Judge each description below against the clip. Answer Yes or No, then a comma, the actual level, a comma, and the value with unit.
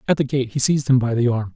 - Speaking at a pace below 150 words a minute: No, fast, 345 wpm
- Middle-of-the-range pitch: No, low, 130 Hz